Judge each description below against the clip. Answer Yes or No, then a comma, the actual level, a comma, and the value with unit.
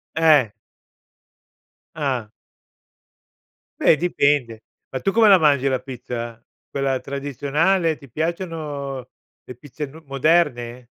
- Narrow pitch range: No, average, 3.9 semitones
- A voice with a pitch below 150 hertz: Yes, medium, 140 Hz